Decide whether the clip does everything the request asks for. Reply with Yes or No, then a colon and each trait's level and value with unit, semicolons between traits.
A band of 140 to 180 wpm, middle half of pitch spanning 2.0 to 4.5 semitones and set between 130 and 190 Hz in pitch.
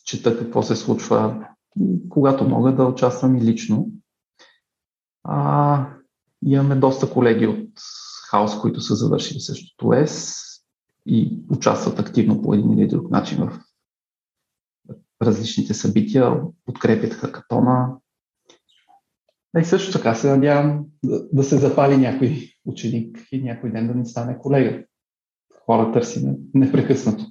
No: average, 125 wpm; average, 3.6 semitones; low, 135 Hz